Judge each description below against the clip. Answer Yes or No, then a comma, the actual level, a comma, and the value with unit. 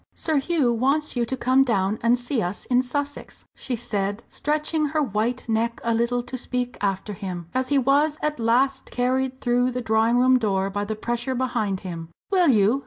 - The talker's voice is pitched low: No, high, 245 Hz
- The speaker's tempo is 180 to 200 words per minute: Yes, average, 195 wpm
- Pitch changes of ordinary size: Yes, average, 3.2 semitones